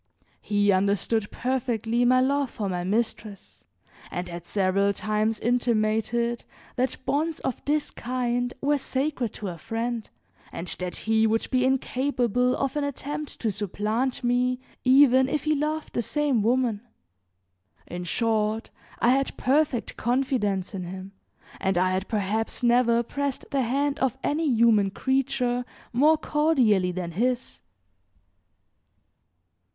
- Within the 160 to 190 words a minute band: No, slow, 135 wpm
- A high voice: Yes, high, 240 Hz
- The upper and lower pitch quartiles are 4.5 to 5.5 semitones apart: No, average, 4.0 semitones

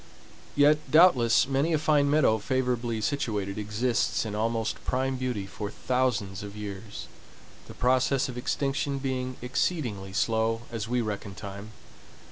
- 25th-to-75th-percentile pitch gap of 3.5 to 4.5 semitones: Yes, average, 4.0 semitones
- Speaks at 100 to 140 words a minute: Yes, slow, 135 wpm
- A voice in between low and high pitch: No, low, 120 Hz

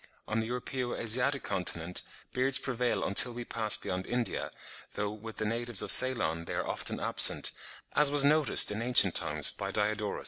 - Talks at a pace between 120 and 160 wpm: No, average, 175 wpm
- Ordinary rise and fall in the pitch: Yes, average, 3.3 semitones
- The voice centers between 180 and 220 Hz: No, low, 115 Hz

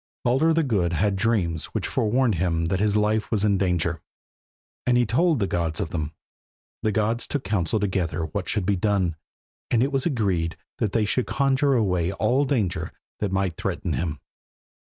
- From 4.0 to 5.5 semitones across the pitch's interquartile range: Yes, average, 5.0 semitones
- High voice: No, low, 100 Hz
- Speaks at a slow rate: No, average, 180 wpm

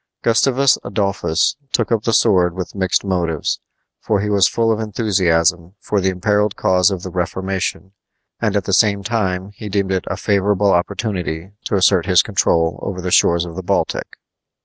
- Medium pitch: No, very low, 95 Hz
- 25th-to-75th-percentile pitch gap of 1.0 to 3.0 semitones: Yes, narrow, 2.4 semitones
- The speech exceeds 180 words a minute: No, average, 175 wpm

